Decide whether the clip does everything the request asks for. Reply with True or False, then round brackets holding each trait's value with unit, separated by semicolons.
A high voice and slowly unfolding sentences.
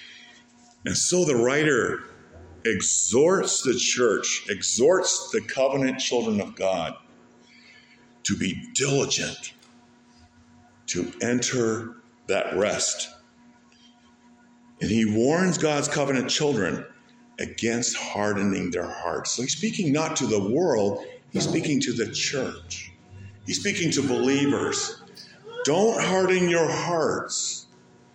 False (135 Hz; 105 wpm)